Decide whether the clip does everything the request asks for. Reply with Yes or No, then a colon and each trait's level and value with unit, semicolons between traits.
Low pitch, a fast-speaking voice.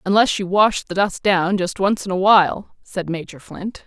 No: high, 190 Hz; fast, 215 wpm